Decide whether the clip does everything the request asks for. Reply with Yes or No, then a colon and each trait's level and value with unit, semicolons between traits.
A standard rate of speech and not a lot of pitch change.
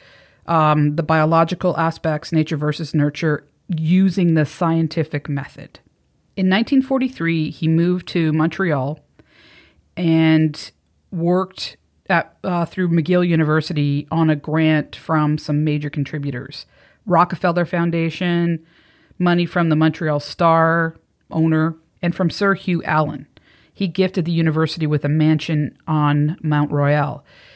No: slow, 120 wpm; narrow, 2.2 semitones